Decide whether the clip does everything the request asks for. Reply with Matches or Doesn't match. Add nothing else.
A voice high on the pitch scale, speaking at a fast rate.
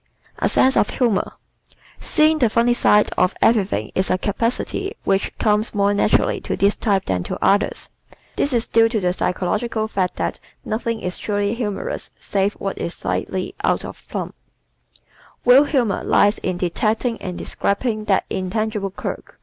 Doesn't match